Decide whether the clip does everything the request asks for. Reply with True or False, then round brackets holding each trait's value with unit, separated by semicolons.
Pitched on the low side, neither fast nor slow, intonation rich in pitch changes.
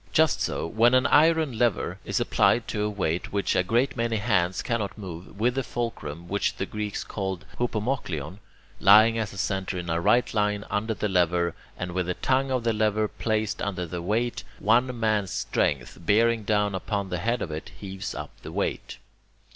False (105 Hz; 195 wpm; 4.0 semitones)